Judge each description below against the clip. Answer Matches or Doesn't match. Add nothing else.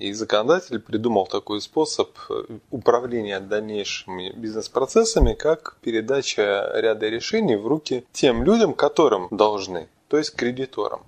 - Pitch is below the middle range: Matches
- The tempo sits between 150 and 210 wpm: Doesn't match